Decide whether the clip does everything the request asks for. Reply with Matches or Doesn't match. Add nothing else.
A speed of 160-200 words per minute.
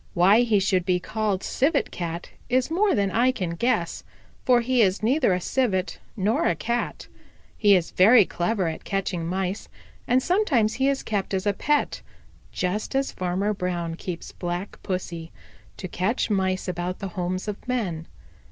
Matches